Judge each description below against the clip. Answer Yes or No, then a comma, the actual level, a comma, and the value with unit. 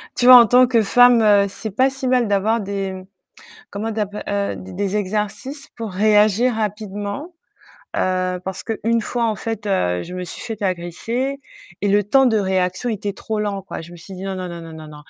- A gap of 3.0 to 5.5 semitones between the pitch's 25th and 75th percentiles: Yes, average, 3.3 semitones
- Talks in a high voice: Yes, high, 205 Hz